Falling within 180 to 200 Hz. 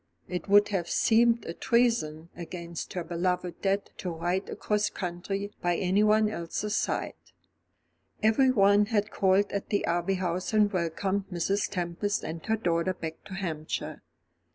Yes: high, 190 Hz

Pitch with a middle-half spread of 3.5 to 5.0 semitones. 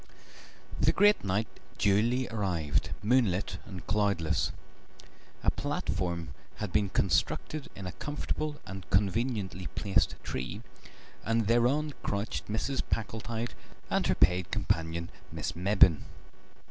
Yes: average, 4.2 semitones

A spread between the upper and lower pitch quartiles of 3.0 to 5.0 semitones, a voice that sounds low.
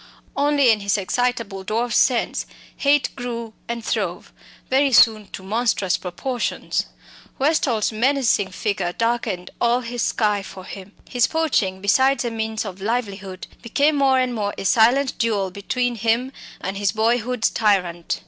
No: average, 3.8 semitones; high, 225 Hz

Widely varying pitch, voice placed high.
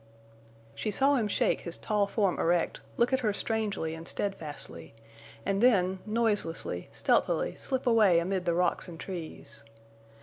No: average, 4.5 semitones; high, 200 Hz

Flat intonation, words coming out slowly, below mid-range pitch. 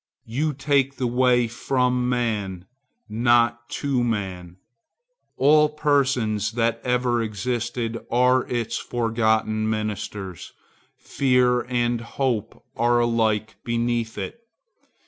Yes: narrow, 2.3 semitones; slow, 100 wpm; low, 120 Hz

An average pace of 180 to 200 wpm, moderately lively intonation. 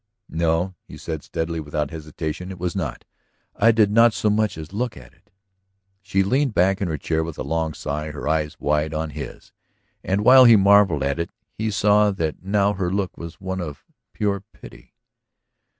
Yes: average, 190 wpm; average, 4.5 semitones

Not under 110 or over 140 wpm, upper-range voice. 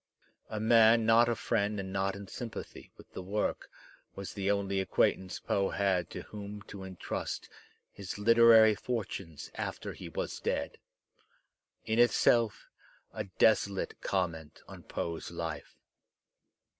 No: slow, 135 wpm; low, 100 Hz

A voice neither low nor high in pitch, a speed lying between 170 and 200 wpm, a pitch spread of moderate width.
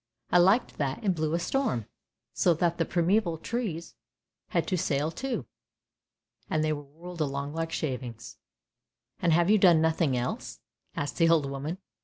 Yes: medium, 165 Hz; average, 175 wpm; average, 3.7 semitones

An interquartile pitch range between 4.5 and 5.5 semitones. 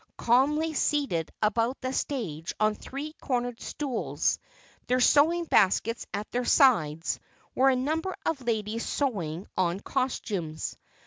Yes: average, 5.2 semitones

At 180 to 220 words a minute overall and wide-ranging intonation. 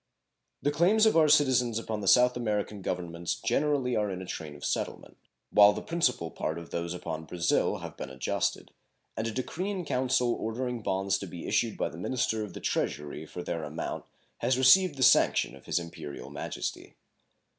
Yes: average, 190 wpm; wide, 6.9 semitones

